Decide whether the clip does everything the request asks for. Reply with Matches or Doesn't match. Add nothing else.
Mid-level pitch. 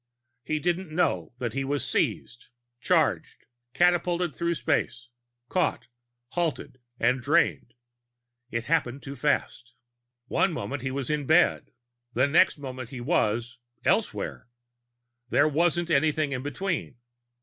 Matches